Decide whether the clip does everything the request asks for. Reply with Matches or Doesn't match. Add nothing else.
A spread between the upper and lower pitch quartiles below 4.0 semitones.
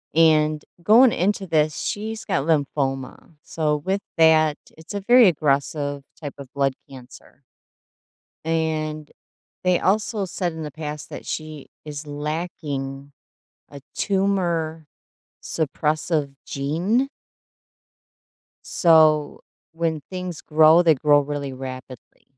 Matches